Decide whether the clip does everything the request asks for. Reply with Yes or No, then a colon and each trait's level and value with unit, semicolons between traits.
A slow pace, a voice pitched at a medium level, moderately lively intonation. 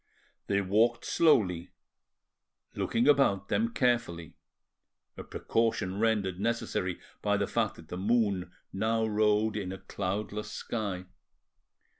No: slow, 115 wpm; low, 105 Hz; average, 3.3 semitones